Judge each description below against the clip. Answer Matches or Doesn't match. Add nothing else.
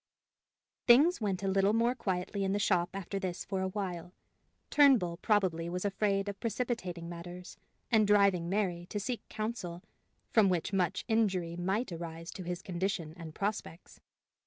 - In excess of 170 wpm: Doesn't match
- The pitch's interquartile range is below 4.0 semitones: Matches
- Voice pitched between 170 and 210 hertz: Matches